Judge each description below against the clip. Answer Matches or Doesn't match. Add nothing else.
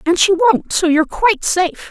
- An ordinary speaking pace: Doesn't match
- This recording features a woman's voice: Matches